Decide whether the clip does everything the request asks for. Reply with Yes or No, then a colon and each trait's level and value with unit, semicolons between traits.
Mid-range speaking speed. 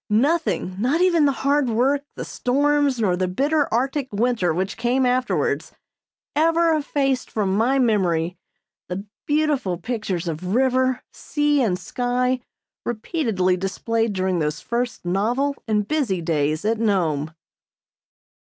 No: slow, 130 wpm